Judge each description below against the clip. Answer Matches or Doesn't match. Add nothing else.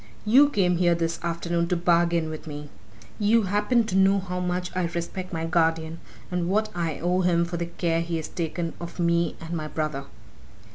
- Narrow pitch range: Matches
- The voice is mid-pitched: Matches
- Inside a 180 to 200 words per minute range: Matches